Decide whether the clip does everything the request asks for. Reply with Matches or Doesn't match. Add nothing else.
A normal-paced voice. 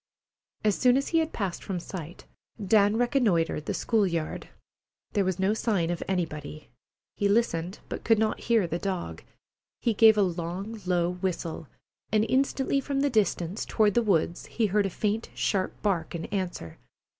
Matches